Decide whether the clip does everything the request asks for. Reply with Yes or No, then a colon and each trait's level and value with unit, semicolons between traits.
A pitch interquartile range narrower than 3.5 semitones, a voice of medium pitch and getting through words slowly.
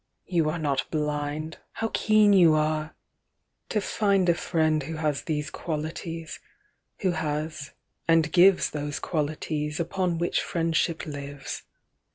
Yes: narrow, 2.4 semitones; medium, 160 Hz; slow, 130 wpm